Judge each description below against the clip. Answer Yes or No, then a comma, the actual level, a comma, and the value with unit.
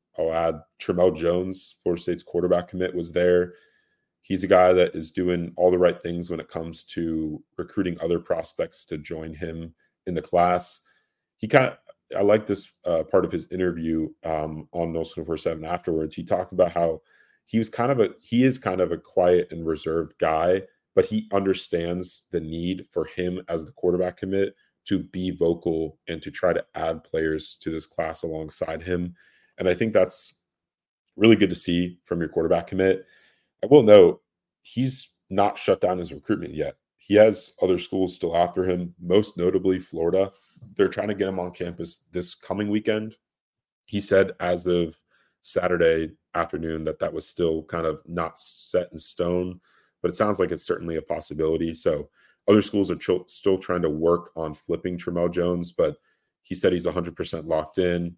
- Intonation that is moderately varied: No, narrow, 2.1 semitones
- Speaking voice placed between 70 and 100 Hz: Yes, very low, 90 Hz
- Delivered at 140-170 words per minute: No, average, 185 wpm